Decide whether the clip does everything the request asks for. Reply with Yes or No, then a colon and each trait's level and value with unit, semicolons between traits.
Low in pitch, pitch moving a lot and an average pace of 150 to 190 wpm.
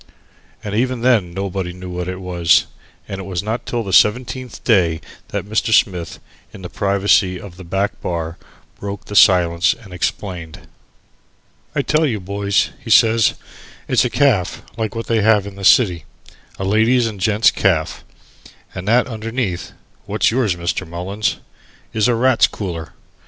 No: low, 100 Hz; average, 3.7 semitones; average, 160 wpm